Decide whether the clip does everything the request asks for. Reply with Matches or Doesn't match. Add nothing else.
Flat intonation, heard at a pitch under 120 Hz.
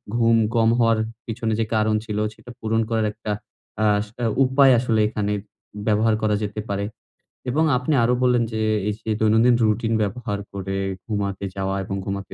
Matches